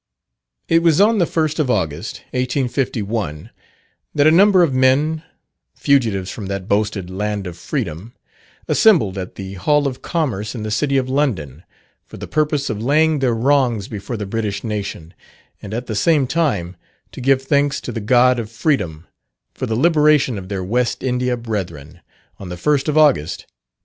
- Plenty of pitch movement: Yes, wide, 6.5 semitones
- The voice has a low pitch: Yes, low, 120 Hz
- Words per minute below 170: No, average, 175 wpm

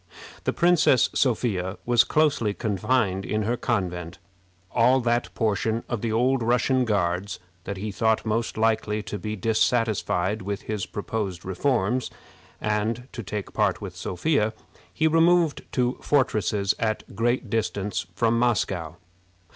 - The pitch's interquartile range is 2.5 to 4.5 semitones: Yes, average, 3.4 semitones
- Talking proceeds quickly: No, average, 140 wpm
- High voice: No, low, 110 Hz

